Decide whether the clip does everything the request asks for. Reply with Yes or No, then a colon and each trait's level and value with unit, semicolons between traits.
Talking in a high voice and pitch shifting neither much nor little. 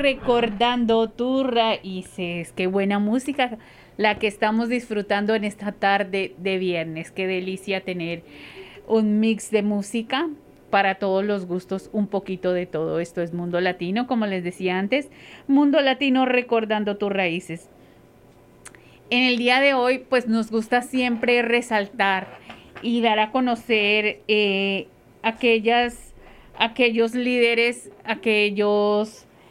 Yes: high, 215 Hz; average, 3.7 semitones